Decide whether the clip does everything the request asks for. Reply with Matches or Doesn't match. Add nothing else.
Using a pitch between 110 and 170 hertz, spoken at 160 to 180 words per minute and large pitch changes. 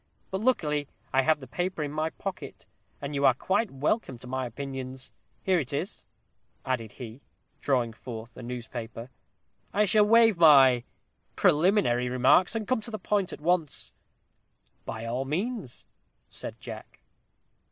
Doesn't match